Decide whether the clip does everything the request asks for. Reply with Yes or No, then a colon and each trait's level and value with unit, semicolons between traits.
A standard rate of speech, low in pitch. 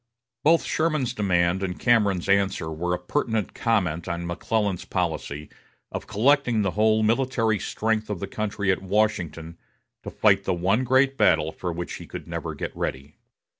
Yes: average, 165 wpm; low, 100 Hz